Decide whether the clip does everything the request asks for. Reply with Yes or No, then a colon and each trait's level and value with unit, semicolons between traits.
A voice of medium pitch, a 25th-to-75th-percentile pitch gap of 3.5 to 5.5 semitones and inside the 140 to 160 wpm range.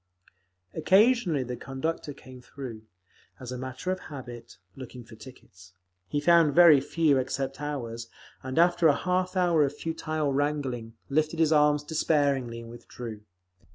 Yes: medium, 145 Hz; average, 4.2 semitones; average, 145 wpm